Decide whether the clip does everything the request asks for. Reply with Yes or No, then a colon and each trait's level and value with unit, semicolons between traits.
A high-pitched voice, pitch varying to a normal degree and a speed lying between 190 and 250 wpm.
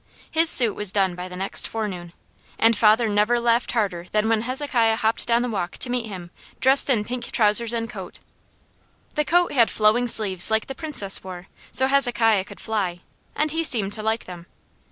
Yes: high, 220 Hz; average, 3.6 semitones; average, 195 wpm